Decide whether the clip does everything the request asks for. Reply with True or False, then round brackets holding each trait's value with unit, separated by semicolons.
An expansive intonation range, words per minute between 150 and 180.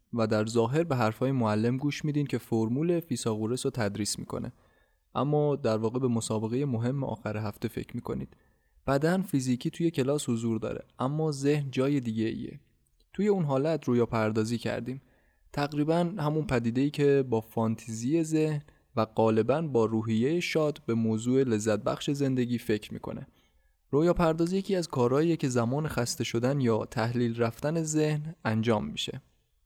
False (4.8 semitones; 155 wpm)